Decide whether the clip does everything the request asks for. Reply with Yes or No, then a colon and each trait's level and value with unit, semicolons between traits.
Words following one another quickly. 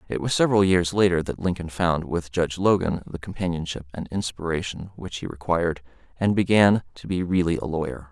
No: average, 185 wpm